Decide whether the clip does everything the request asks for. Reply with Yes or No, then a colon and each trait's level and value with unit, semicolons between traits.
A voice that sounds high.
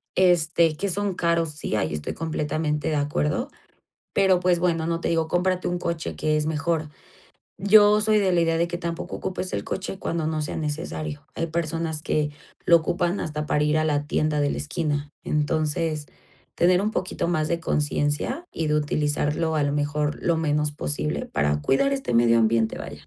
No: medium, 155 Hz